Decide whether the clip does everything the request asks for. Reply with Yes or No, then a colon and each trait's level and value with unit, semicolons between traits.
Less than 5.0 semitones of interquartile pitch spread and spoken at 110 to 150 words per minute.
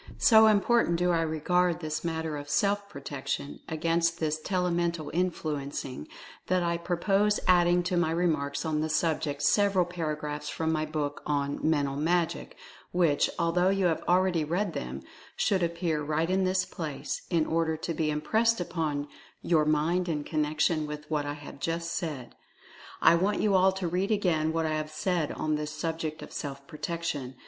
No: average, 2.7 semitones; average, 175 wpm